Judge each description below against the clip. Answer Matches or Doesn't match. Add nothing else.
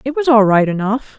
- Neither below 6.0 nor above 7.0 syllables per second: Doesn't match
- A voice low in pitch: Doesn't match